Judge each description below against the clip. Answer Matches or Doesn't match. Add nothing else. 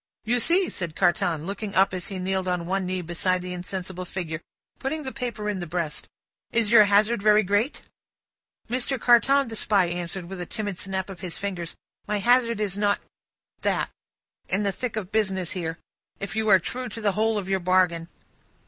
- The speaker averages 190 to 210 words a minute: Matches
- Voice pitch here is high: Matches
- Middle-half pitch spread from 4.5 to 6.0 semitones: Doesn't match